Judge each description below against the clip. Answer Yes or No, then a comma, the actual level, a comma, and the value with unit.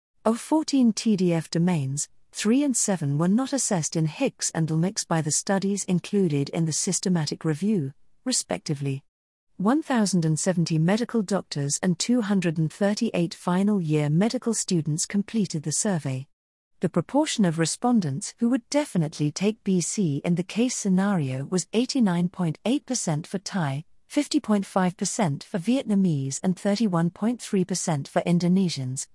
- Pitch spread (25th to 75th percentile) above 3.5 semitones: Yes, average, 5.0 semitones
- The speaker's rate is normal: No, slow, 120 wpm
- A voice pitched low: No, medium, 185 Hz